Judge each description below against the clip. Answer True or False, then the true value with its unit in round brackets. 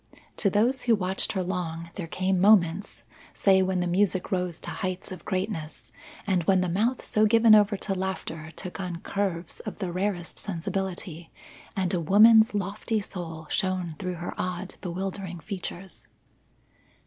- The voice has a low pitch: False (185 Hz)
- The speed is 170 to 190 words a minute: False (155 wpm)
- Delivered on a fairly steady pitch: True (2.3 semitones)